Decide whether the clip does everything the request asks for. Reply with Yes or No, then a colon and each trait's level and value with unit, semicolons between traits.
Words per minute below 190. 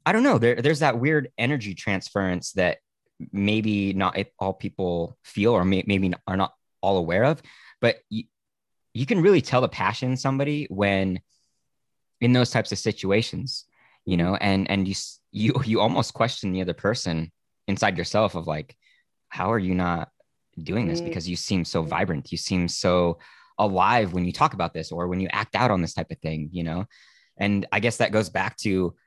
No: average, 195 wpm